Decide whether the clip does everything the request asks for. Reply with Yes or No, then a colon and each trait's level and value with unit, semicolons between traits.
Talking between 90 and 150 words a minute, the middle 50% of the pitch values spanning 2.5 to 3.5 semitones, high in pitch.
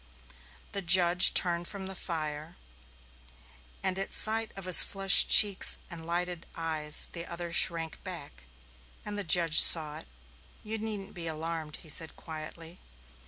No: average, 145 wpm; average, 2.8 semitones; medium, 170 Hz